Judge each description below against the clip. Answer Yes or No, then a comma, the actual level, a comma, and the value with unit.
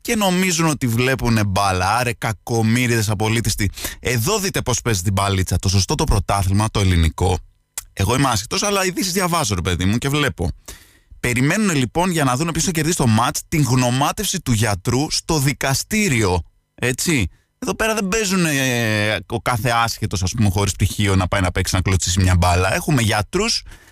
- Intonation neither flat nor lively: No, wide, 7.0 semitones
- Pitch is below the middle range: Yes, low, 115 Hz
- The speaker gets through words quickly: Yes, fast, 175 wpm